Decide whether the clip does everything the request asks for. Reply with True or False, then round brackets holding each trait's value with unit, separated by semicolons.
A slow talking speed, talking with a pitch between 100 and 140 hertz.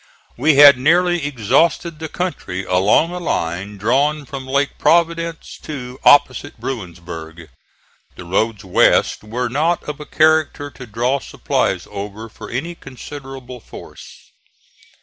True (130 wpm; 135 Hz)